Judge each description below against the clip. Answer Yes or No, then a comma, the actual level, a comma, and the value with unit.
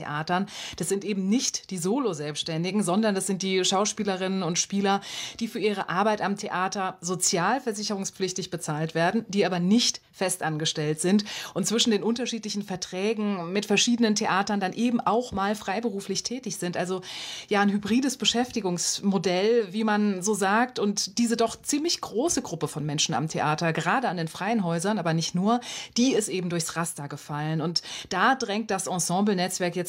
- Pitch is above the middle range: Yes, high, 195 Hz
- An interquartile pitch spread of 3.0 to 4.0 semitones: Yes, average, 3.3 semitones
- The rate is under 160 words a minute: No, average, 170 wpm